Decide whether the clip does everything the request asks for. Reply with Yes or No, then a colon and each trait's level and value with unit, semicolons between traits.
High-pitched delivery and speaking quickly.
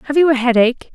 Yes: very high, 265 Hz; fast, 255 wpm